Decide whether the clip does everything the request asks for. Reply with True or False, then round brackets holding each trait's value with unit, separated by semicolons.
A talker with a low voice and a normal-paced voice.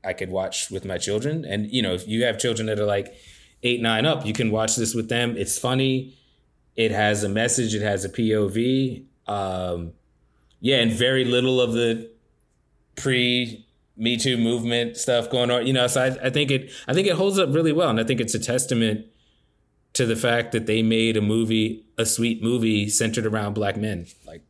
False (115 Hz; 210 wpm)